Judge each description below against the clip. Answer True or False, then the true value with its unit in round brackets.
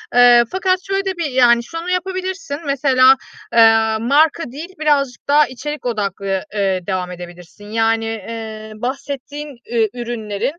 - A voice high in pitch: True (245 Hz)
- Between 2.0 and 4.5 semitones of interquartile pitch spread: False (5.2 semitones)